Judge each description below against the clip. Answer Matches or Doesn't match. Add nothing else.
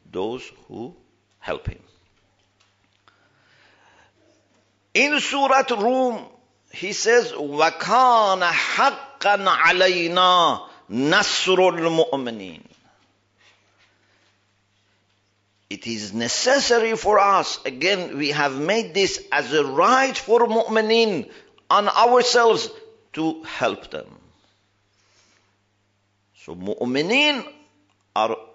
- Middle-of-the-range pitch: Matches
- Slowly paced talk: Matches